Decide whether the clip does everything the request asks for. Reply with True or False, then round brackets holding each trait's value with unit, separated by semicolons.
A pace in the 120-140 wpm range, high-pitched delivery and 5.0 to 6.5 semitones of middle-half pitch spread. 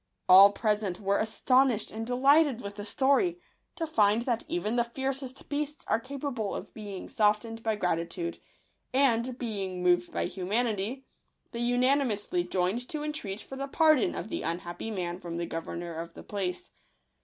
False (160 wpm; 225 Hz; 5.6 semitones)